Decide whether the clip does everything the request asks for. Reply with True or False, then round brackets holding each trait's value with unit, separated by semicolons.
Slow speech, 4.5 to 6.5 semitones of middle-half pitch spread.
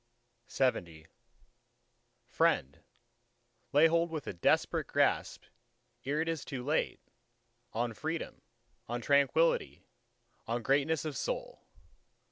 True (100 wpm; 5.2 semitones)